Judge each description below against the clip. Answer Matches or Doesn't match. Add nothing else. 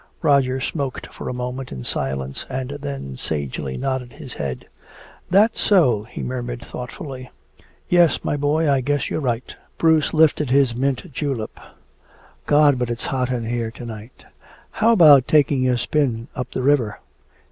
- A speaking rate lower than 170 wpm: Matches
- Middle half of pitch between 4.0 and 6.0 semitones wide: Doesn't match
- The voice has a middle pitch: Doesn't match